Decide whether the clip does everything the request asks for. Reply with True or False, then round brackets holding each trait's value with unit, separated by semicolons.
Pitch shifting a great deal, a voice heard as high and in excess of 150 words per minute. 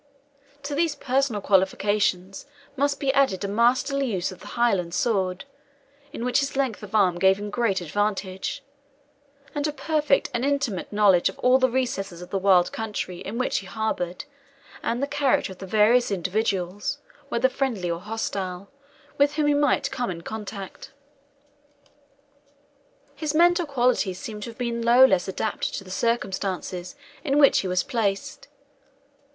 True (5.8 semitones; 220 Hz; 160 wpm)